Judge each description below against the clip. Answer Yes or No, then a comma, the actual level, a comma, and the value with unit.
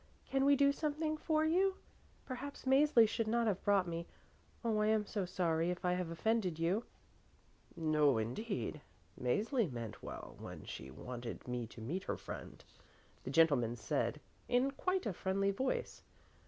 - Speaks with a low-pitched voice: No, high, 195 Hz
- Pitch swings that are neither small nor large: No, wide, 8.4 semitones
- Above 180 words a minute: No, average, 160 wpm